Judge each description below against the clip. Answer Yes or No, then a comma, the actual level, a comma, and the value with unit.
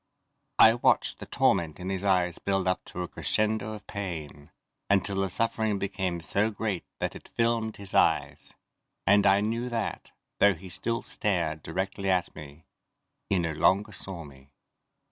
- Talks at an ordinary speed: Yes, average, 165 wpm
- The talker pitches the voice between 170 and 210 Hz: No, very low, 95 Hz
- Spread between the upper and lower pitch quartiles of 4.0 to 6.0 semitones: No, average, 3.2 semitones